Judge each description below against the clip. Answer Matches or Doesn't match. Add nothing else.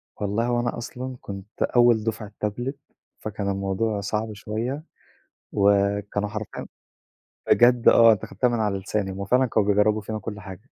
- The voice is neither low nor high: Doesn't match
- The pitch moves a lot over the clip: Doesn't match